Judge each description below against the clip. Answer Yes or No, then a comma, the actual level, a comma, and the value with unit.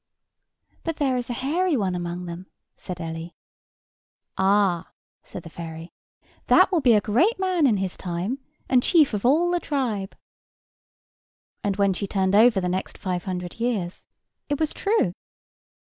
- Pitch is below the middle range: No, high, 205 Hz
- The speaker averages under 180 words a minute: Yes, average, 160 wpm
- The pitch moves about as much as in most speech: No, wide, 7.1 semitones